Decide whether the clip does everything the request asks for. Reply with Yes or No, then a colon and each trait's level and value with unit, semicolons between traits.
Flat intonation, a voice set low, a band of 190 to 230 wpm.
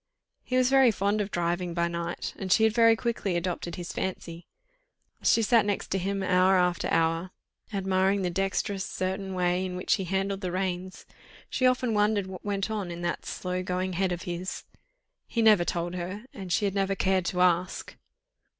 No: narrow, 2.2 semitones; high, 190 Hz; average, 195 wpm